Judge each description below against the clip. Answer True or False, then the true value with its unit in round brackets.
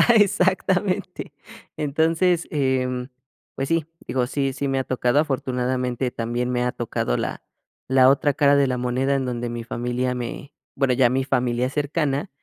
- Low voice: True (130 Hz)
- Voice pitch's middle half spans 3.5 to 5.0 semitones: False (2.6 semitones)